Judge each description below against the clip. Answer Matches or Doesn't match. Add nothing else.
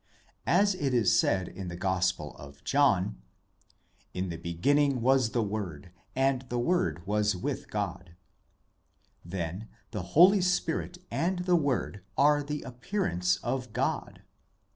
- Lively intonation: Matches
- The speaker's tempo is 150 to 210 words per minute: Doesn't match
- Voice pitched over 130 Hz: Doesn't match